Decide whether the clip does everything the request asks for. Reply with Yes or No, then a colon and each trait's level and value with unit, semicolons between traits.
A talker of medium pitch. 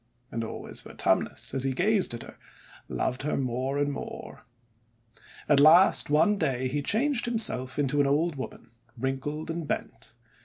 Yes: medium, 145 Hz